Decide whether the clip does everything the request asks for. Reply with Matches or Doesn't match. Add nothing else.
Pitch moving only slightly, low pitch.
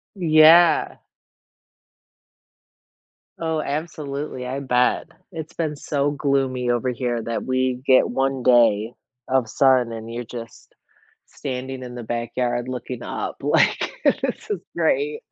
Doesn't match